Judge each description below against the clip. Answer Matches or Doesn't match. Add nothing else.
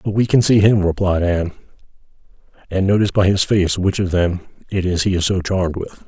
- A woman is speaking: Doesn't match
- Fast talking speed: Matches